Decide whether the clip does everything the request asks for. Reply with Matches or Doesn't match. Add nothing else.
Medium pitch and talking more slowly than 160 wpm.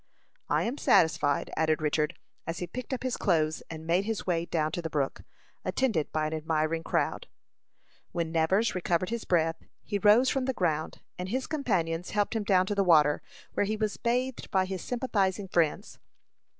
Doesn't match